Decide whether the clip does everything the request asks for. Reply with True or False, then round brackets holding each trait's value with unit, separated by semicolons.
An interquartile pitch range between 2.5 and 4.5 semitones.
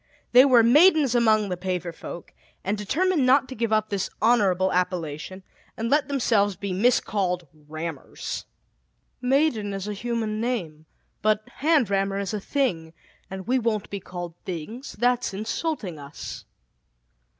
False (5.1 semitones)